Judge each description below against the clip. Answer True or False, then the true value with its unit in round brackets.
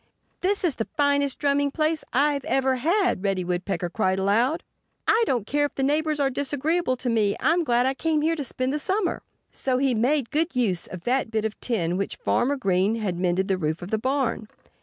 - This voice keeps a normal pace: False (215 wpm)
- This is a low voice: False (260 Hz)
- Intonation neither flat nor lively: False (6.2 semitones)